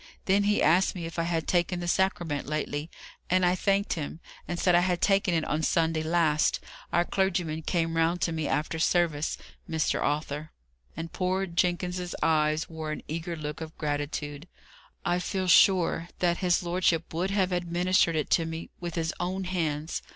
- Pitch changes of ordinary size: No, narrow, 2.2 semitones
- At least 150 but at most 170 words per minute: No, average, 180 wpm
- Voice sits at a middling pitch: Yes, medium, 170 Hz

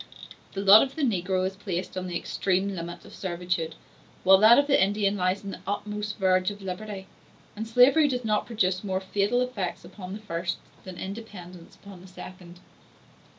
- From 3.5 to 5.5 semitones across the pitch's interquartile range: No, narrow, 2.4 semitones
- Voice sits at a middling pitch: No, high, 195 Hz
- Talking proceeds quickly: No, average, 185 wpm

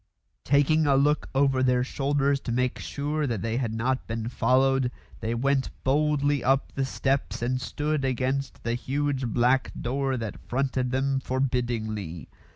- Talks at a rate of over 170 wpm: No, average, 150 wpm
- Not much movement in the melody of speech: Yes, narrow, 2.2 semitones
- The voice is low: Yes, low, 130 Hz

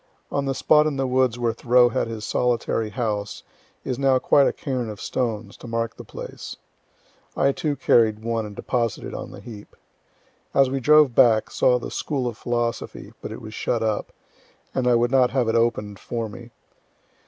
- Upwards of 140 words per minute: Yes, average, 190 wpm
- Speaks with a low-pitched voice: Yes, low, 120 Hz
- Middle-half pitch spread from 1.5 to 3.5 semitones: Yes, narrow, 2.5 semitones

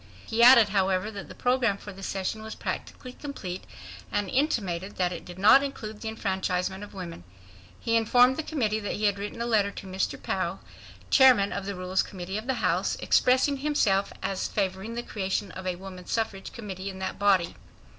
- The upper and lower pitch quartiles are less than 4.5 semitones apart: Yes, average, 3.5 semitones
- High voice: Yes, high, 200 Hz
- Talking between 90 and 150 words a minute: No, average, 195 wpm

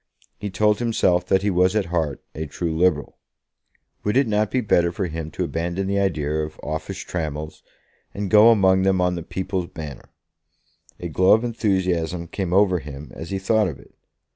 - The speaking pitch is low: Yes, very low, 90 Hz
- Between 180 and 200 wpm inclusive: Yes, average, 190 wpm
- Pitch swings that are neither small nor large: Yes, average, 3.5 semitones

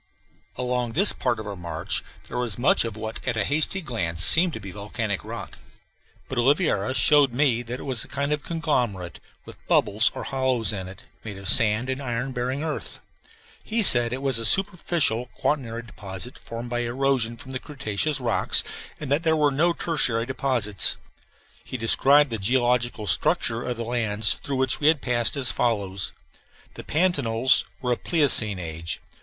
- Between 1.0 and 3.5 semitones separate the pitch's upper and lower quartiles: No, average, 3.9 semitones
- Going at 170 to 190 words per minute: Yes, average, 180 wpm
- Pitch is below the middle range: Yes, low, 125 Hz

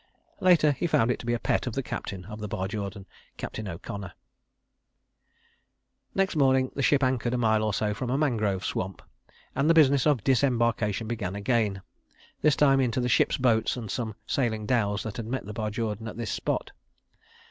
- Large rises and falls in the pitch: No, average, 3.9 semitones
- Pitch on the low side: Yes, low, 115 Hz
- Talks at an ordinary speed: Yes, average, 185 wpm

